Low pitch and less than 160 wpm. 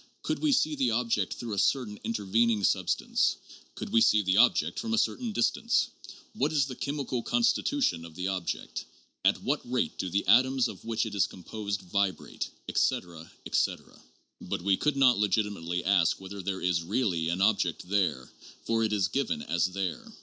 No: low, 105 Hz; average, 185 wpm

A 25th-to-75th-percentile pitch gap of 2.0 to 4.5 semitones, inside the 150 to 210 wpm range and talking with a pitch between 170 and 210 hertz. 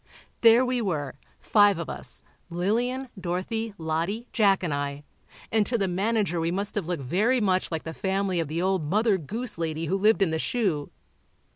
No: average, 4.9 semitones; average, 175 wpm; high, 190 Hz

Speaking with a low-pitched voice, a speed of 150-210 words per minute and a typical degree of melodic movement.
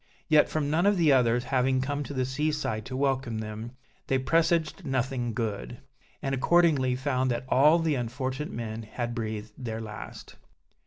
Yes: low, 130 Hz; average, 170 wpm; average, 3.9 semitones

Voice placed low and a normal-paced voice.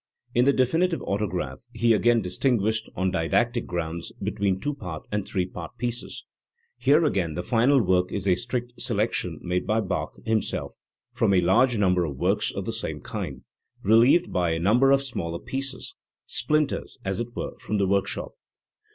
Yes: low, 105 Hz; average, 170 wpm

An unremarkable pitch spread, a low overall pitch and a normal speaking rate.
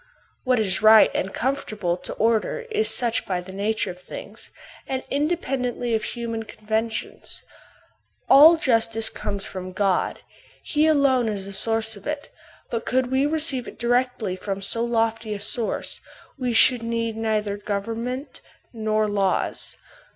No: average, 3.2 semitones; high, 225 Hz; average, 150 wpm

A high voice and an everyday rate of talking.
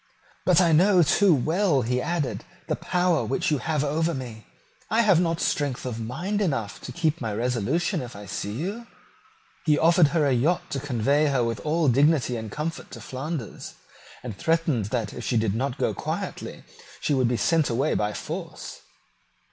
No: medium, 145 Hz; average, 185 wpm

